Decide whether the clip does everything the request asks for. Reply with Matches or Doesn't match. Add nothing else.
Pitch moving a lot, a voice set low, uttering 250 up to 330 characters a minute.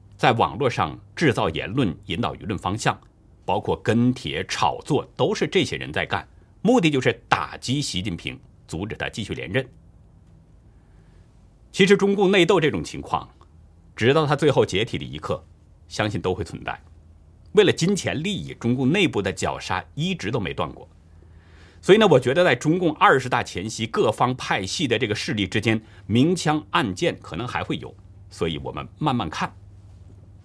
Matches